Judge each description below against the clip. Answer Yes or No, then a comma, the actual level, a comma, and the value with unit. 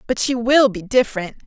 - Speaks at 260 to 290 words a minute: No, fast, 205 wpm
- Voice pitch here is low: No, high, 230 Hz